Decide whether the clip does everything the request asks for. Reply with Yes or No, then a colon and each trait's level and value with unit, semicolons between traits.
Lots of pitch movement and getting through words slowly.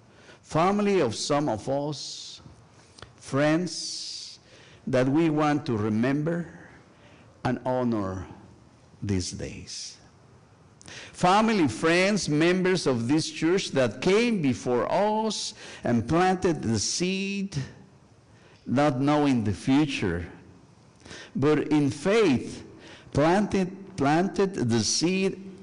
Yes: wide, 6.9 semitones; slow, 95 wpm